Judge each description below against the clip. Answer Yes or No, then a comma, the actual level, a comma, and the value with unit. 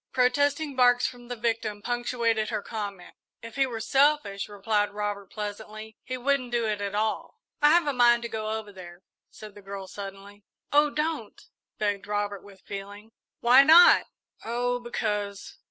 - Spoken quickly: No, average, 165 wpm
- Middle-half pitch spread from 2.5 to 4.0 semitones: Yes, average, 3.3 semitones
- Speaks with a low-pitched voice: No, high, 220 Hz